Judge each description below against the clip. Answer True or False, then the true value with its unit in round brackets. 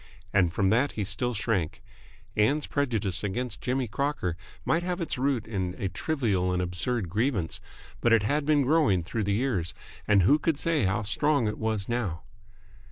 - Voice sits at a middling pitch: False (110 Hz)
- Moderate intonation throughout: False (6.4 semitones)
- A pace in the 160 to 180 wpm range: True (175 wpm)